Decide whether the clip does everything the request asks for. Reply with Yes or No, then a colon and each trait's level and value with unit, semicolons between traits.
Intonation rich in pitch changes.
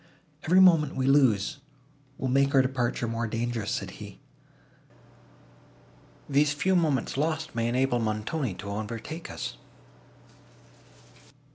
No: average, 4.6 semitones